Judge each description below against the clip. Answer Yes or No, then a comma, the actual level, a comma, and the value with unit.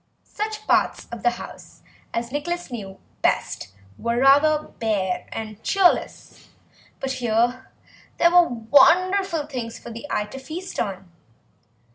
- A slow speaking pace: Yes, slow, 130 wpm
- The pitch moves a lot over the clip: Yes, wide, 6.9 semitones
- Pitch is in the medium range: No, very high, 255 Hz